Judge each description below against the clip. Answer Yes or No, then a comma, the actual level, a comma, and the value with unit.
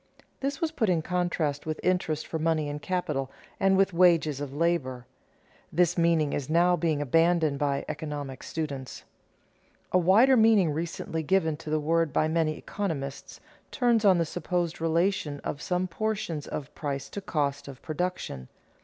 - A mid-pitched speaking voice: Yes, medium, 165 Hz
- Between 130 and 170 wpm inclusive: Yes, average, 160 wpm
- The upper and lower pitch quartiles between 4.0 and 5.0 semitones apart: No, average, 3.5 semitones